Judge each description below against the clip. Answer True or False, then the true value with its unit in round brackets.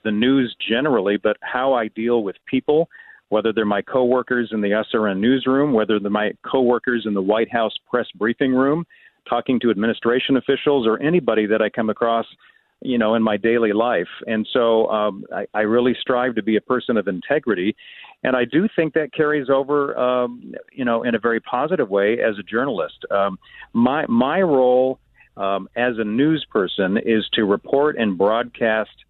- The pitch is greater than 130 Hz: False (115 Hz)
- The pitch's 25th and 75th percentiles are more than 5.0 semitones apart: False (3.2 semitones)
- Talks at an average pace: True (190 wpm)